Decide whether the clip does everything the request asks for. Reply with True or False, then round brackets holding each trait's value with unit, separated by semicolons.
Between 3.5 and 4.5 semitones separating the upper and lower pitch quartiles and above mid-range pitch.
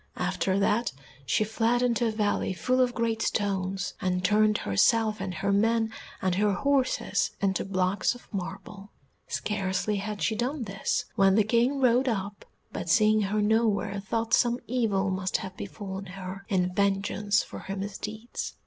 False (2.7 semitones; 205 Hz)